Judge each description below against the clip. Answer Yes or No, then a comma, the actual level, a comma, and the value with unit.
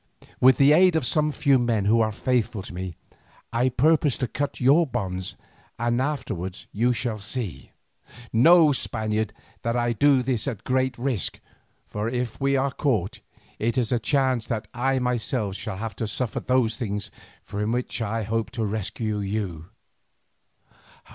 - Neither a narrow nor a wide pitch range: Yes, average, 3.4 semitones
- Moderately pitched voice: No, low, 120 Hz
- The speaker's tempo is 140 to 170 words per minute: Yes, average, 165 wpm